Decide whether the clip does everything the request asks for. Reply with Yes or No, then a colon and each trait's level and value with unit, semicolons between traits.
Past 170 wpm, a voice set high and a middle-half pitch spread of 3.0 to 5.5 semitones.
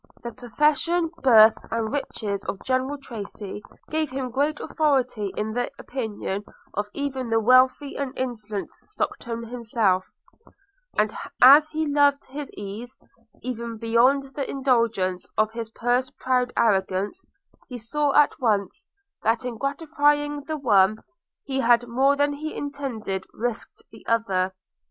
No: slow, 135 wpm; high, 245 Hz; average, 4.4 semitones